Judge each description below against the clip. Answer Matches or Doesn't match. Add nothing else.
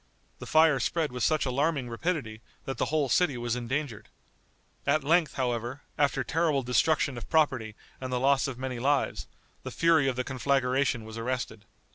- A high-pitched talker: Doesn't match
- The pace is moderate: Matches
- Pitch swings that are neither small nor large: Matches